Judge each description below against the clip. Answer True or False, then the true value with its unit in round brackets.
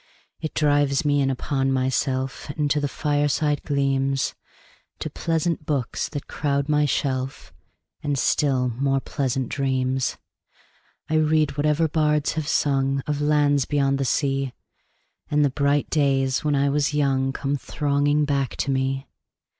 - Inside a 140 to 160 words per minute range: True (150 wpm)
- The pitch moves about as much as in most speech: False (1.6 semitones)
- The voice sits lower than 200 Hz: True (140 Hz)